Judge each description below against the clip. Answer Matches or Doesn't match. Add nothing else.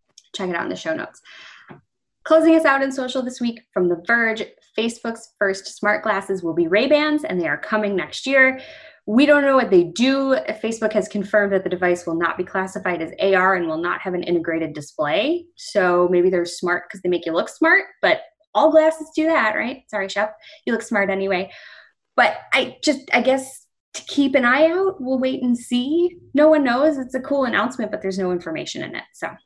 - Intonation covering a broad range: Matches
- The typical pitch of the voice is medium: Doesn't match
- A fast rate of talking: Matches